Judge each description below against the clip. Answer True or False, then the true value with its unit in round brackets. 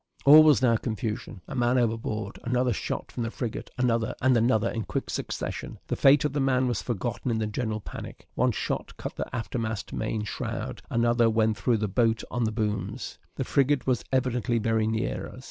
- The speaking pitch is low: True (115 Hz)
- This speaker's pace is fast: False (195 wpm)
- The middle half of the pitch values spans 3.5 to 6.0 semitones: False (2.4 semitones)